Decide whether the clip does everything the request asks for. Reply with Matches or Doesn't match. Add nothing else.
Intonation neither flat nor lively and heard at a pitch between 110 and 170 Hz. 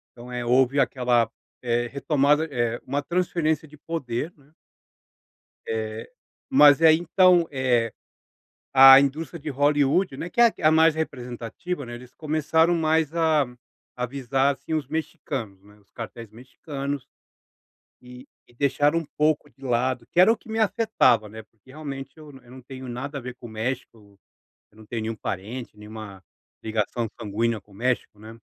Matches